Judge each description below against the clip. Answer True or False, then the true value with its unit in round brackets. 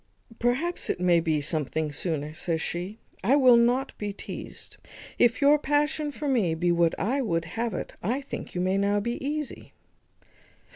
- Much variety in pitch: True (7.8 semitones)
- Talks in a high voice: True (205 Hz)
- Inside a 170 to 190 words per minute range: True (175 wpm)